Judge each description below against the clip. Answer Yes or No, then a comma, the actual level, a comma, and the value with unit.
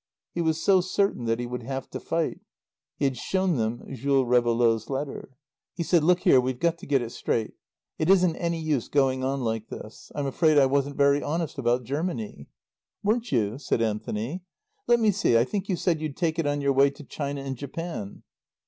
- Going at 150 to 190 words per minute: No, fast, 205 wpm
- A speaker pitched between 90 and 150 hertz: Yes, medium, 140 Hz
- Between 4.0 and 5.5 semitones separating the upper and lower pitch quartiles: Yes, average, 5.2 semitones